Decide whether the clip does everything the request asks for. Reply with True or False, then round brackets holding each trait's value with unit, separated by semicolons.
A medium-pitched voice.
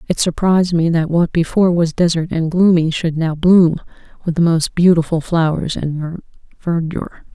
True (165 Hz)